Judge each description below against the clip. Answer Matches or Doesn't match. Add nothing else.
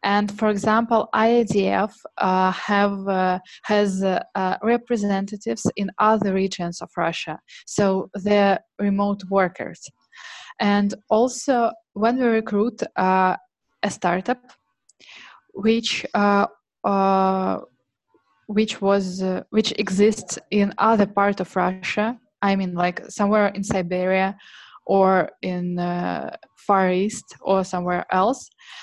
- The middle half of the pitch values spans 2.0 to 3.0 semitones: Matches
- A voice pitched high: Matches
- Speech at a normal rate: Doesn't match